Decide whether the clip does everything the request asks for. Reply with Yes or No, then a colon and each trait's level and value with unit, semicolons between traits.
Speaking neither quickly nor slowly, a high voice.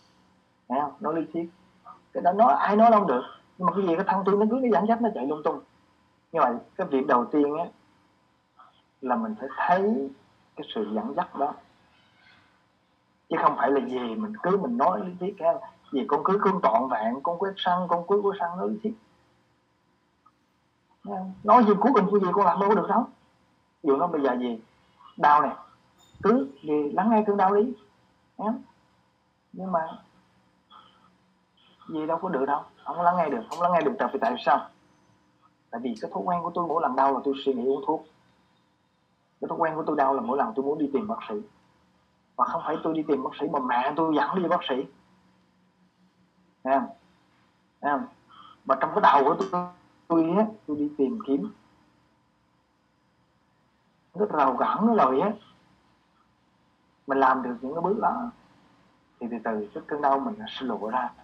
No: average, 200 wpm; medium, 160 Hz